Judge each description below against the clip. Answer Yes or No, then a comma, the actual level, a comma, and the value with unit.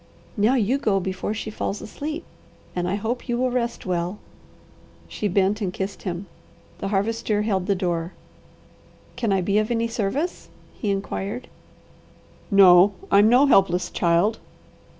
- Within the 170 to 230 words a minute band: No, average, 150 wpm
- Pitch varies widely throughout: No, average, 3.3 semitones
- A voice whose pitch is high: Yes, high, 205 Hz